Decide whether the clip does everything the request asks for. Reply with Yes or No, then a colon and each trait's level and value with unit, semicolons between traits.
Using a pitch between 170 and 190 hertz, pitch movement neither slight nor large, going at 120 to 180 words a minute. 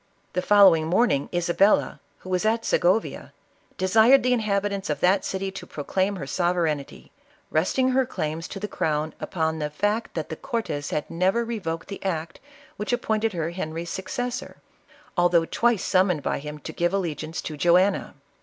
Yes: medium, 185 Hz; average, 4.4 semitones; average, 170 wpm